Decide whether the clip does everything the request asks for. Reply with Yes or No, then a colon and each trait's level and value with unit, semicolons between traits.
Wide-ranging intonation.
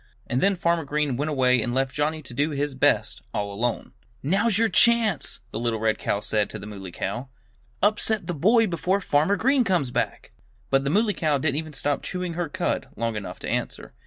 Yes: wide, 7.2 semitones